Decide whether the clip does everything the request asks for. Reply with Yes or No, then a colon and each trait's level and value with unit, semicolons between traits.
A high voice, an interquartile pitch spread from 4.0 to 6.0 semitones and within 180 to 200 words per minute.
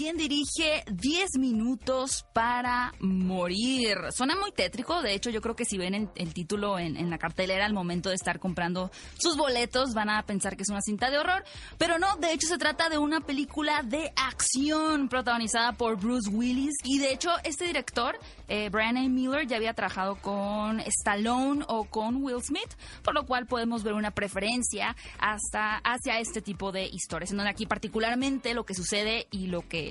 Yes: high, 230 Hz; average, 5.1 semitones; fast, 190 wpm